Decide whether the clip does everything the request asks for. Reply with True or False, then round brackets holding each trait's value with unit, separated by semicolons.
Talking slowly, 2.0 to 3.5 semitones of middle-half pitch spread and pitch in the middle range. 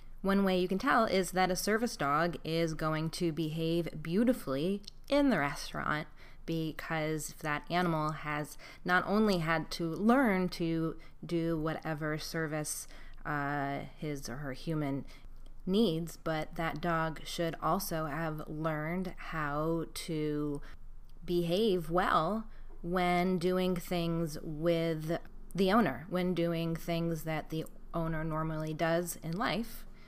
True (130 wpm; 2.6 semitones; 165 Hz)